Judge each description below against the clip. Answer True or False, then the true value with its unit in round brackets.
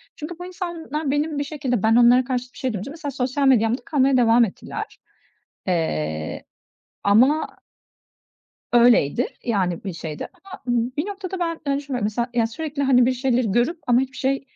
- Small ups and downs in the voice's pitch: False (3.9 semitones)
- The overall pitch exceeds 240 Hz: True (255 Hz)